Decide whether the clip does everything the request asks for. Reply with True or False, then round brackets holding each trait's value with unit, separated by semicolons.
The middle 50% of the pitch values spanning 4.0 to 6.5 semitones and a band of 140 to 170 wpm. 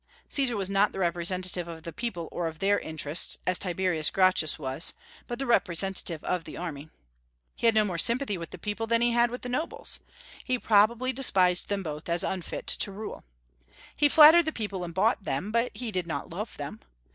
False (5.4 semitones; 205 wpm)